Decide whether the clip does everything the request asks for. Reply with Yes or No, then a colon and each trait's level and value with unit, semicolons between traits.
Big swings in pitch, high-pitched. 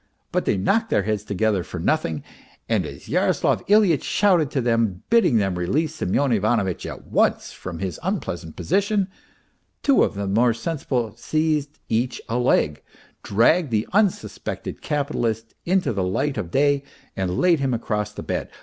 No: wide, 7.4 semitones; low, 120 Hz